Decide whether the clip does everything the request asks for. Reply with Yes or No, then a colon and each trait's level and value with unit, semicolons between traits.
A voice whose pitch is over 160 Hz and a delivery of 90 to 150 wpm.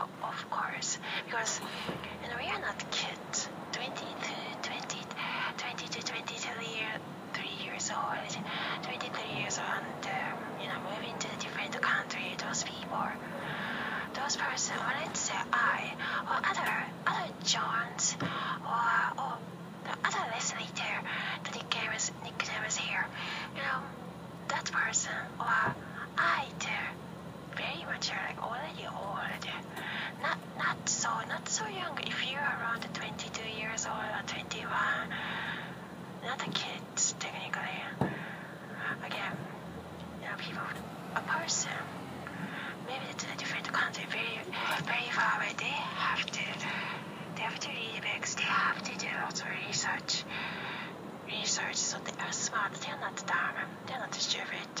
Yes: high, 190 Hz; average, 140 wpm